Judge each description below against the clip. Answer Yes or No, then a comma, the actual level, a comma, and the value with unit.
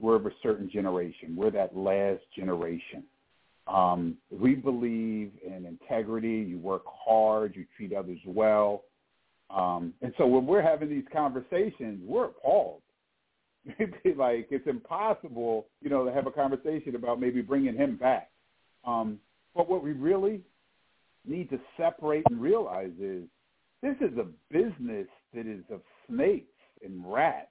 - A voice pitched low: Yes, low, 120 Hz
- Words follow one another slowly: No, average, 145 wpm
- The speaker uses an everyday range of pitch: No, wide, 7.8 semitones